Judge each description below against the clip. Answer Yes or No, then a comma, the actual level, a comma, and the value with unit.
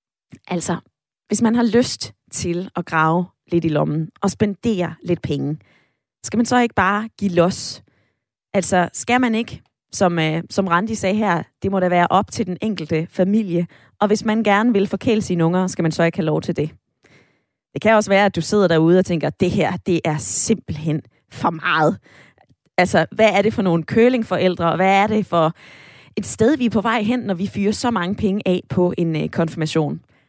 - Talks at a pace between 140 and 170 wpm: No, average, 205 wpm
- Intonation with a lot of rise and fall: No, average, 4.0 semitones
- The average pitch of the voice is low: No, medium, 185 Hz